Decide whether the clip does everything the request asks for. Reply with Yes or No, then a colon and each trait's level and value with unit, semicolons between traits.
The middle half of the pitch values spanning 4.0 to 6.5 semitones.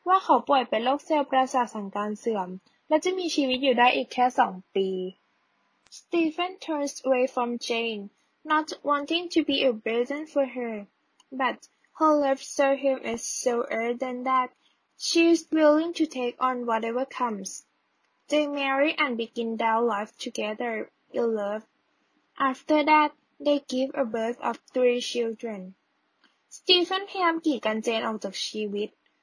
Yes: average, 4.6 semitones